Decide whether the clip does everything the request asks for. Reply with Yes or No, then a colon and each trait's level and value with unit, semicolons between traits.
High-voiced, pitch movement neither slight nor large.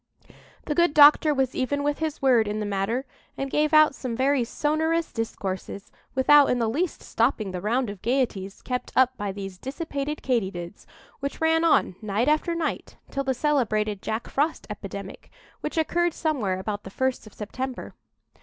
No: very high, 260 Hz; wide, 6.0 semitones